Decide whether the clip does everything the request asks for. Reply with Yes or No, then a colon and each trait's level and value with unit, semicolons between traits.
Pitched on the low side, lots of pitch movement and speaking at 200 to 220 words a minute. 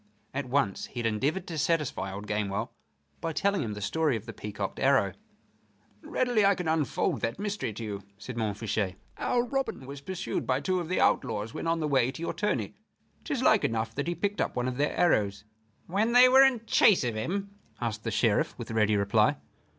Yes: low, 130 Hz; wide, 8.4 semitones; fast, 205 wpm